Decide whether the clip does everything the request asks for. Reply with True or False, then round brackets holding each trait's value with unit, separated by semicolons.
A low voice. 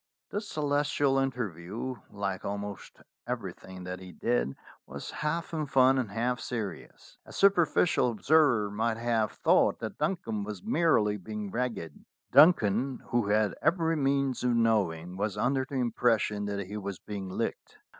True (115 Hz)